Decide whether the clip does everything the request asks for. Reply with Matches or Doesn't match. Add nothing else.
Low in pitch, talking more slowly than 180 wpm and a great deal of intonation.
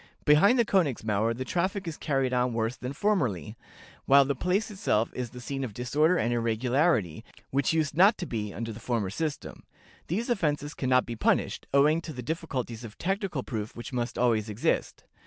Doesn't match